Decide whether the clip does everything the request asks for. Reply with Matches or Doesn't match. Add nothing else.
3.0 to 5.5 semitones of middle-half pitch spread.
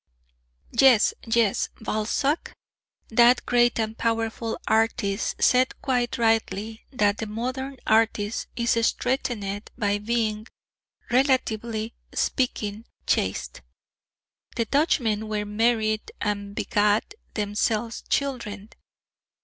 Doesn't match